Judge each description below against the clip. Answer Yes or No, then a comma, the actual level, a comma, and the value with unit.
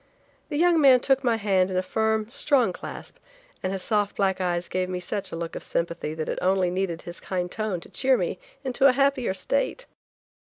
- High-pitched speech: Yes, high, 200 Hz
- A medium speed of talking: No, fast, 210 wpm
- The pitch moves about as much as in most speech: No, wide, 6.1 semitones